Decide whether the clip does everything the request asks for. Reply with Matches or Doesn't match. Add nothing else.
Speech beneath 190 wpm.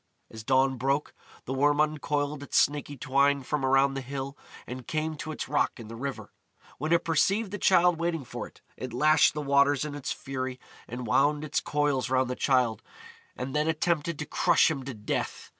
Doesn't match